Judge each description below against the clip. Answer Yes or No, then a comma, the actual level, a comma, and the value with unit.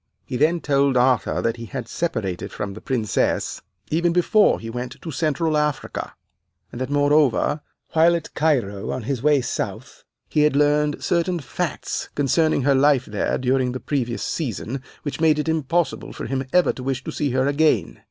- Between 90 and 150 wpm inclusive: No, average, 180 wpm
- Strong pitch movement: No, average, 3.5 semitones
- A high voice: No, medium, 140 Hz